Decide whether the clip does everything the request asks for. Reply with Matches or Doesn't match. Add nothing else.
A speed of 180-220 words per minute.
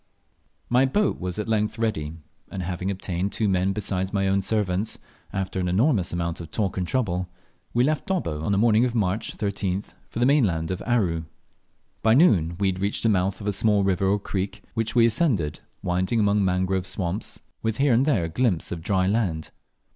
Matches